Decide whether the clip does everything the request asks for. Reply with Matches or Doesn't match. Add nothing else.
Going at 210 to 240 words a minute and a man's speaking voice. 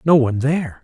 Matches